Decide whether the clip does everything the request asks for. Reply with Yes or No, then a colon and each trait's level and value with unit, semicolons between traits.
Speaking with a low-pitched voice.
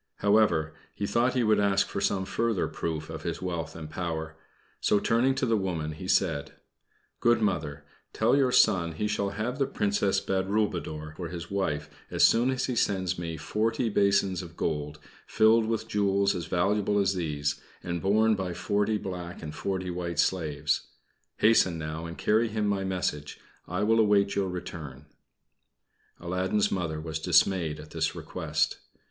Yes: very low, 95 Hz